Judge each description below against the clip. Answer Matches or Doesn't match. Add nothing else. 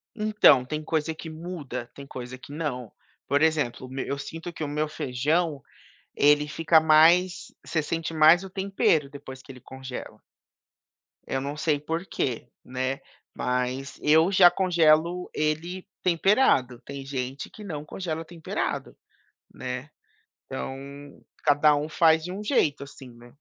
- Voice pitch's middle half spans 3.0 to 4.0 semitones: Matches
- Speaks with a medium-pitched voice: Matches